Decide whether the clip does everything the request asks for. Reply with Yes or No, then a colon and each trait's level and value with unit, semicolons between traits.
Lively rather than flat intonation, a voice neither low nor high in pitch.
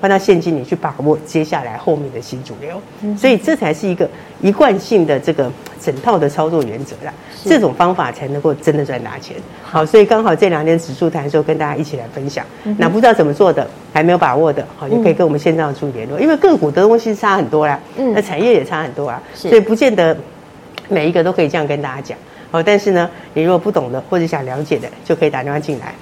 No: average, 4.9 semitones; medium, 165 Hz